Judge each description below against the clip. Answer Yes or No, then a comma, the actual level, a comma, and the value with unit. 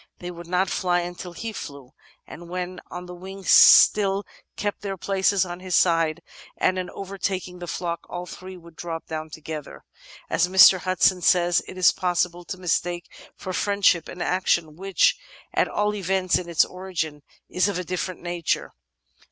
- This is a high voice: No, medium, 180 Hz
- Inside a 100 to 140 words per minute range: No, average, 170 wpm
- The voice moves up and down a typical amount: No, narrow, 1.5 semitones